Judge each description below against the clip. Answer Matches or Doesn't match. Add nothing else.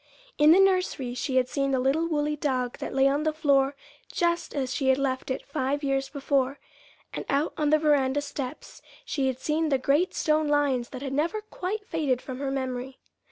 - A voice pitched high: Matches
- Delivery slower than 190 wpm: Doesn't match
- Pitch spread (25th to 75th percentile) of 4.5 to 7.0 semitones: Doesn't match